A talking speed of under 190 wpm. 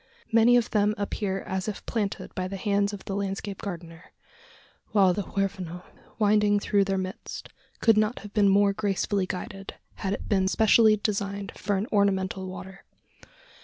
Yes: average, 165 wpm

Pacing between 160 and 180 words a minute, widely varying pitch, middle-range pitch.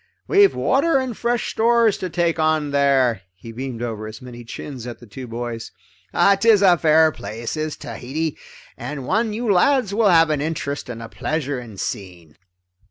Yes: average, 175 wpm; wide, 8.6 semitones; medium, 150 Hz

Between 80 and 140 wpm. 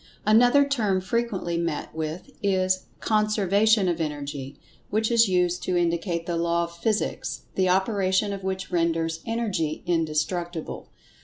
Yes: slow, 135 wpm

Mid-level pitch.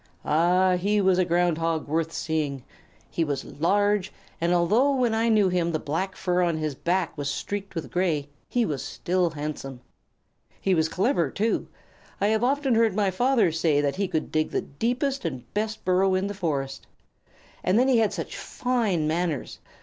Yes: medium, 180 Hz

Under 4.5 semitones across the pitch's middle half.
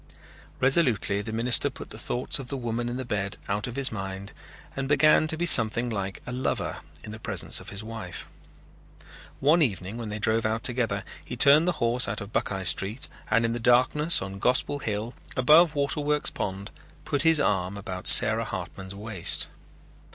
No: average, 5.0 semitones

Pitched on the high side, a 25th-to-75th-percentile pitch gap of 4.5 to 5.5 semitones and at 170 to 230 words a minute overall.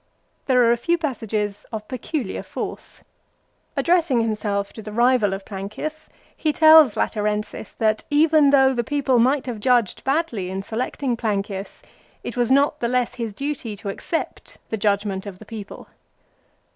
No: high, 235 Hz; average, 4.8 semitones; average, 160 wpm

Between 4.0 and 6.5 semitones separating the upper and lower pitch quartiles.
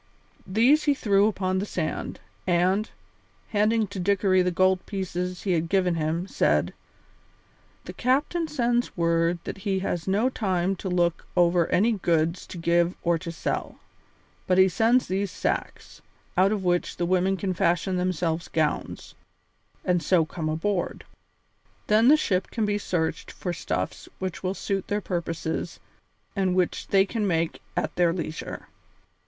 No: average, 2.8 semitones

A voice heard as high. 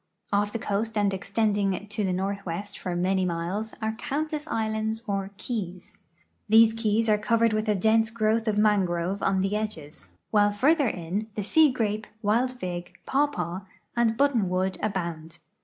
Yes: high, 210 Hz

